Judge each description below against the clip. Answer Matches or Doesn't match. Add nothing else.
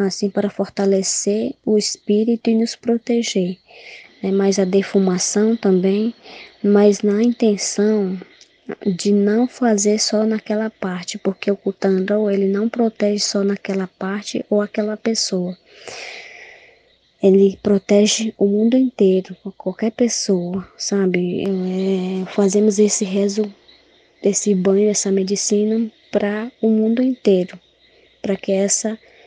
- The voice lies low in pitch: Doesn't match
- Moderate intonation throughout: Doesn't match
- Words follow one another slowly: Matches